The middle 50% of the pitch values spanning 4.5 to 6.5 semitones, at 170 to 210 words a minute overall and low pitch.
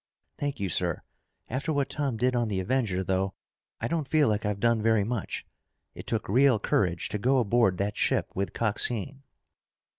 Yes: average, 4.9 semitones; average, 180 wpm; low, 115 Hz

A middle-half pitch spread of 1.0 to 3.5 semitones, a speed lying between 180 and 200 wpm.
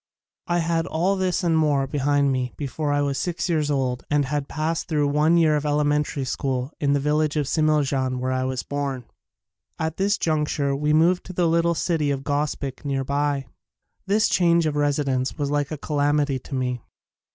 Yes: narrow, 2.5 semitones; average, 190 wpm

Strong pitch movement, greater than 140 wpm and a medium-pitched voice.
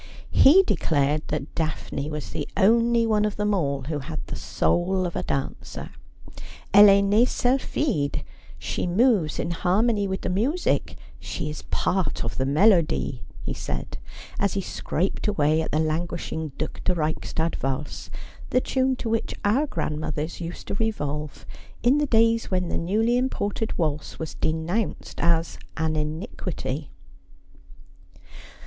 Yes: wide, 6.1 semitones; average, 150 wpm; medium, 175 Hz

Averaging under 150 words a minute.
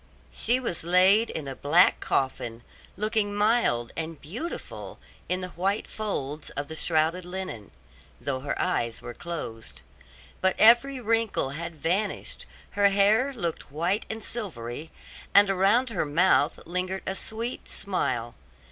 Yes: average, 140 wpm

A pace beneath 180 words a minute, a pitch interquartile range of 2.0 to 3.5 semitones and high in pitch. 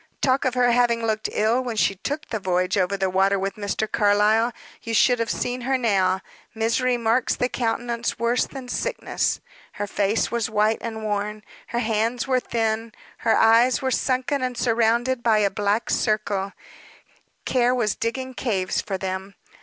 Yes: average, 170 wpm; average, 3.0 semitones; high, 225 Hz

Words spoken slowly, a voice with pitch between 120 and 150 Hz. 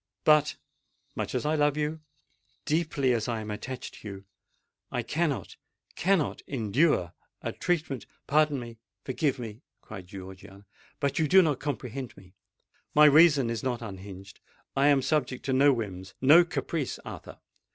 Yes: slow, 130 wpm; low, 135 Hz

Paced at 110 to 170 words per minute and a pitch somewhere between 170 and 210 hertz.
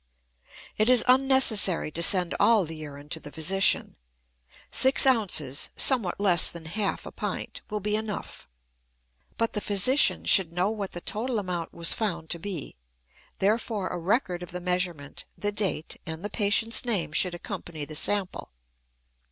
Yes: average, 160 wpm; high, 190 Hz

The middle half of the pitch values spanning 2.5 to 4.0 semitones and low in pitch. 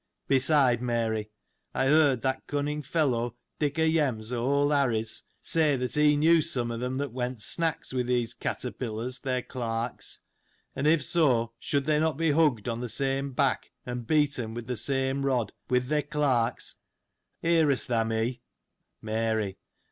Yes: average, 3.6 semitones; low, 130 Hz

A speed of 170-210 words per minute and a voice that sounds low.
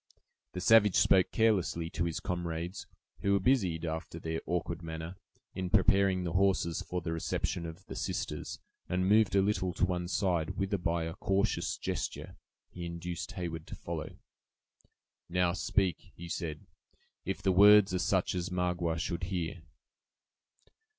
No: average, 155 wpm; very low, 90 Hz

